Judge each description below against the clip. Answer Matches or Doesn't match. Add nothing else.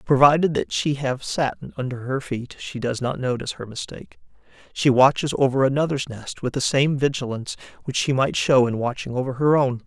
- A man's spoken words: Matches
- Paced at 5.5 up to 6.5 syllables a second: Matches